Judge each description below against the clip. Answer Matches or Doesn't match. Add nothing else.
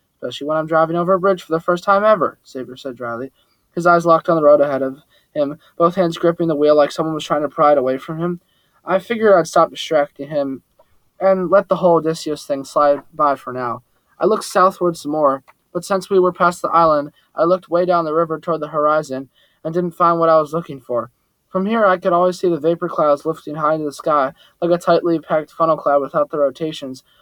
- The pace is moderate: Doesn't match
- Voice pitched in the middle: Matches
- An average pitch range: Matches